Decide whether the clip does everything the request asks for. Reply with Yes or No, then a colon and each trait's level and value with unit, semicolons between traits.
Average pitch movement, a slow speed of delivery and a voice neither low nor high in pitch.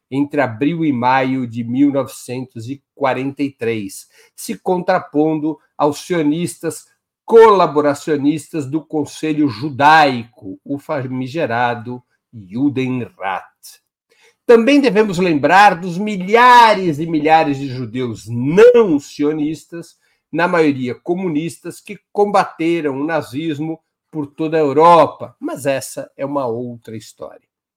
Yes: average, 4.2 semitones; slow, 95 wpm; medium, 150 Hz